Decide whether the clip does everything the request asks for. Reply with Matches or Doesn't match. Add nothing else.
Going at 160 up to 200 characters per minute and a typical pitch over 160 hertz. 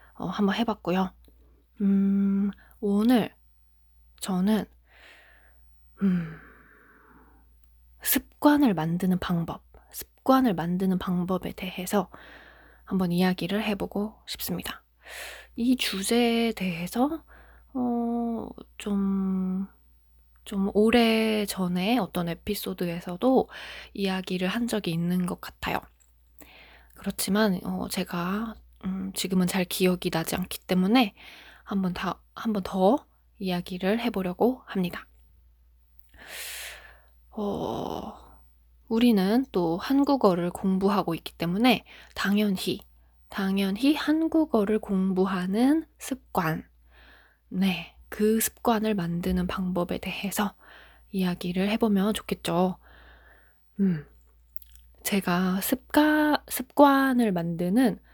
Matches